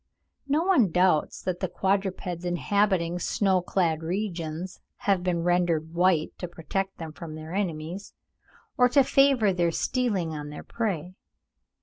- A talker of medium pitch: Yes, medium, 180 Hz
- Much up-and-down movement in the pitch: No, average, 3.1 semitones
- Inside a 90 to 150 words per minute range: Yes, average, 140 wpm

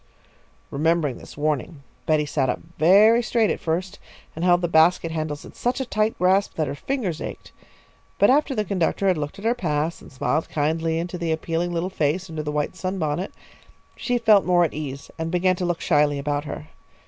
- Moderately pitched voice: Yes, medium, 165 Hz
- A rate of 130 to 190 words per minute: No, average, 200 wpm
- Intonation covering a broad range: No, average, 3.7 semitones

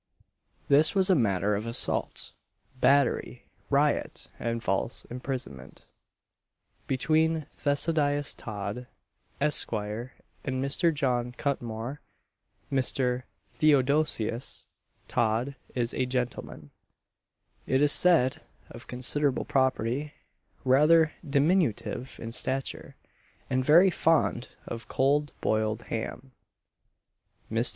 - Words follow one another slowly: Yes, slow, 95 wpm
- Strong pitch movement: No, average, 3.8 semitones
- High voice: No, low, 130 Hz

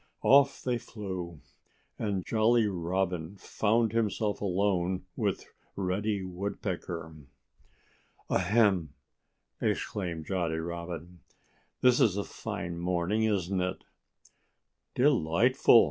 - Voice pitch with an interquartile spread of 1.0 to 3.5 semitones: No, average, 3.9 semitones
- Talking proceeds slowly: Yes, slow, 85 wpm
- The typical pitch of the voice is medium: No, very low, 95 Hz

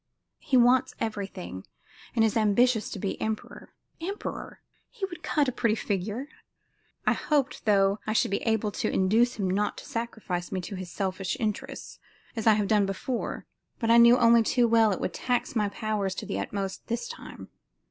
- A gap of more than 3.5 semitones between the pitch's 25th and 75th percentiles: No, average, 3.2 semitones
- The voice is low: No, high, 220 Hz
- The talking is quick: No, average, 185 wpm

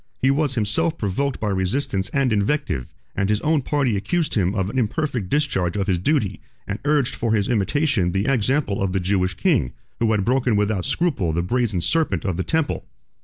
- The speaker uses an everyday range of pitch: No, wide, 6.5 semitones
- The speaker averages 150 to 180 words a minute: No, average, 195 wpm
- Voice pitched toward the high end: No, low, 110 Hz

